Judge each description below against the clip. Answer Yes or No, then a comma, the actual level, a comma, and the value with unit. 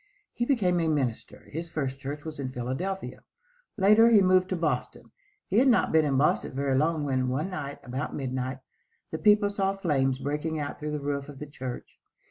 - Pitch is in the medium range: Yes, medium, 150 Hz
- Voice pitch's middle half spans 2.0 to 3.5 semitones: No, average, 5.3 semitones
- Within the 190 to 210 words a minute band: Yes, average, 195 wpm